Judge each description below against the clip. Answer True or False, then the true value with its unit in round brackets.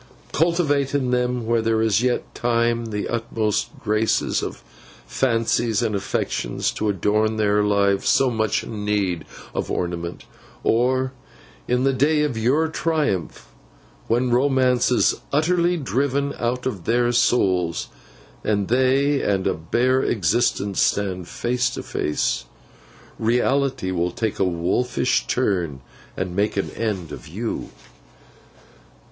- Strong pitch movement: False (4.1 semitones)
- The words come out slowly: True (130 wpm)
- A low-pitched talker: True (115 Hz)